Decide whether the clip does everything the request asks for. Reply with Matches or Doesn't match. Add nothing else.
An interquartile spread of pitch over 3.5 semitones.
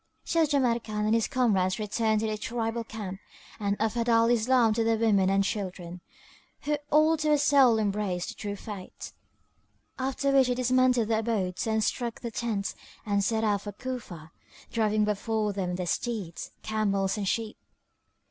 Doesn't match